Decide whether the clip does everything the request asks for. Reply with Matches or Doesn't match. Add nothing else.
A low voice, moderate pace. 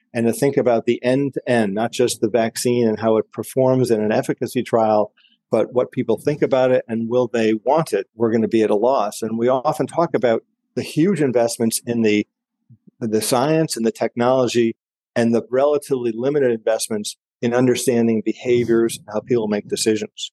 Matches